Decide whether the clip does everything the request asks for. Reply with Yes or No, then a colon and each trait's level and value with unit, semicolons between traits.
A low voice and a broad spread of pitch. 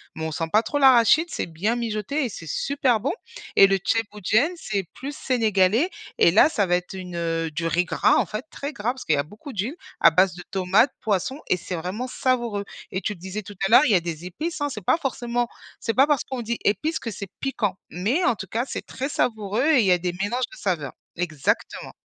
No: high, 210 Hz; wide, 6.0 semitones